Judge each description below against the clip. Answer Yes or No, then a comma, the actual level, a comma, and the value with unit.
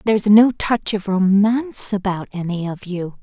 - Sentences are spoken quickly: No, average, 170 wpm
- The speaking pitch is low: No, high, 200 Hz